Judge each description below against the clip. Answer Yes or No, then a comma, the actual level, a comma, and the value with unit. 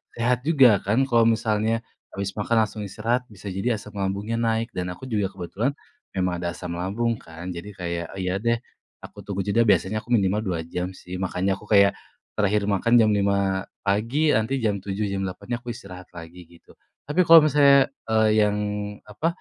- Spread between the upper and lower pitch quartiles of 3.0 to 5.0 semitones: Yes, average, 3.5 semitones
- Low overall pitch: Yes, low, 105 Hz